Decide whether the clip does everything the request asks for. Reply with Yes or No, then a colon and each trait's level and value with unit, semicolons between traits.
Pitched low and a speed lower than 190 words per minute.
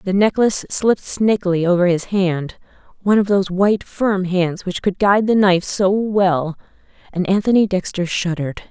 No: high, 190 Hz; average, 150 wpm